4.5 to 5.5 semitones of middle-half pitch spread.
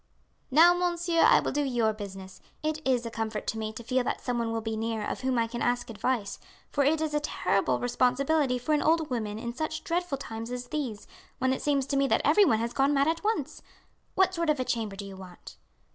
Yes: average, 5.1 semitones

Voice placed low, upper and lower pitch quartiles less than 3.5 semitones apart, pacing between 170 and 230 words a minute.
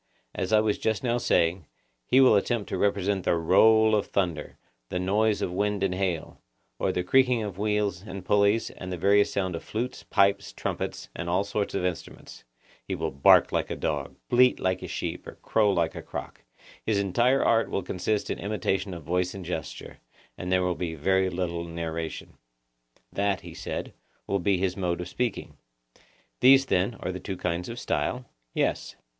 Yes: very low, 95 Hz; average, 2.9 semitones; average, 190 wpm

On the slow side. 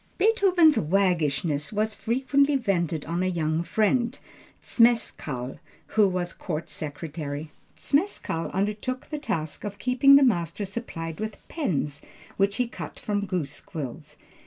Yes: slow, 130 wpm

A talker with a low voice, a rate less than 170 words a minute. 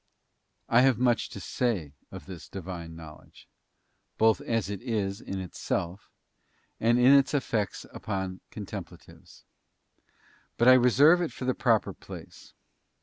Yes: low, 110 Hz; average, 140 wpm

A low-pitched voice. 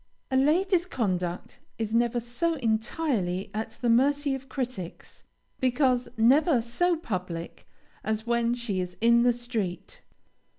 No: high, 240 Hz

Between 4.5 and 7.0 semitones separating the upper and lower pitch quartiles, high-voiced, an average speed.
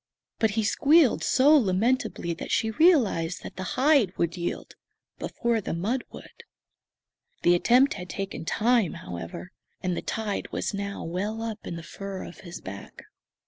Yes: average, 5.3 semitones; high, 200 Hz; average, 160 wpm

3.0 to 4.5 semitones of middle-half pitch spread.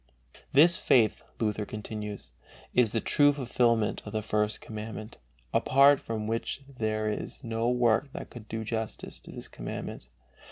No: narrow, 2.4 semitones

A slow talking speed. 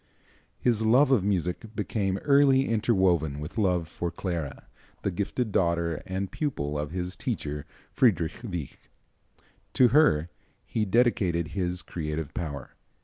Yes: slow, 130 wpm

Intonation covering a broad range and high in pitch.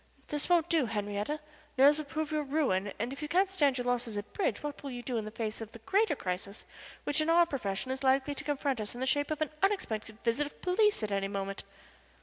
Yes: wide, 5.9 semitones; very high, 270 Hz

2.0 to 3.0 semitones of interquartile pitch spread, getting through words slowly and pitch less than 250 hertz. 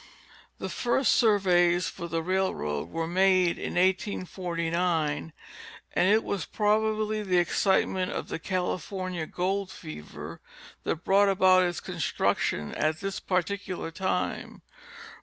Yes: average, 2.7 semitones; slow, 120 wpm; medium, 185 Hz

